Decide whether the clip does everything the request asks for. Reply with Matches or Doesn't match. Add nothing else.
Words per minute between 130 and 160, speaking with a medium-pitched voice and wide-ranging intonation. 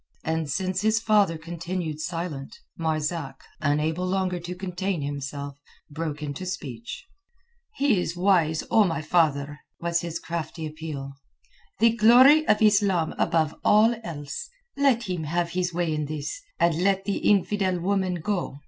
Doesn't match